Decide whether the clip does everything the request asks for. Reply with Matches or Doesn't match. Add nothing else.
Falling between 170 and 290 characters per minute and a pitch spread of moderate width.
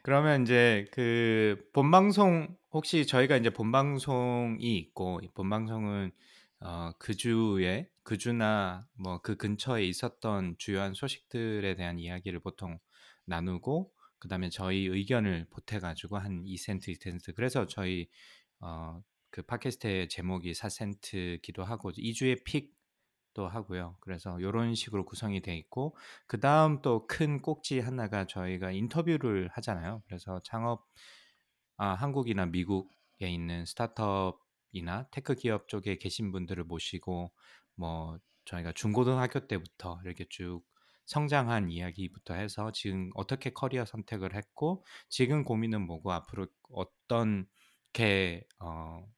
Matches